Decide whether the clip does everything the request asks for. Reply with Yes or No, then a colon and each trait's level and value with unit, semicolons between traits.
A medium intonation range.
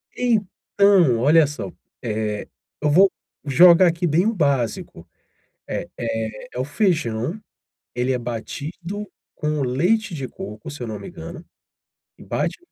No: wide, 6.6 semitones